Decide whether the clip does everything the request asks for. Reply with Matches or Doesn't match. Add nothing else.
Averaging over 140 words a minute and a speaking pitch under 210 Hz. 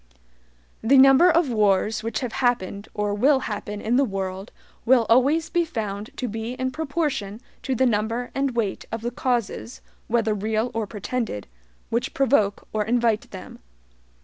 Doesn't match